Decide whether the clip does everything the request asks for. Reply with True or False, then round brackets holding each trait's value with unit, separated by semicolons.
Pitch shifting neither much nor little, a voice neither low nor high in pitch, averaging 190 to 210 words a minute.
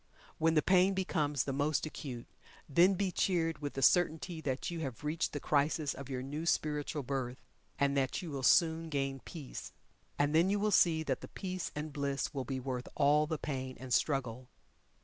True (3.1 semitones; 150 Hz; 195 wpm)